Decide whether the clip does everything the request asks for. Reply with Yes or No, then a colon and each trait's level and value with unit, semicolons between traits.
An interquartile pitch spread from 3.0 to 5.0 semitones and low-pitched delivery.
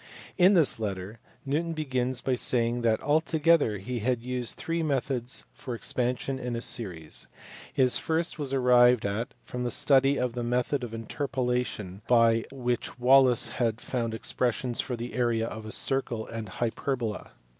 No: narrow, 2.6 semitones; low, 125 Hz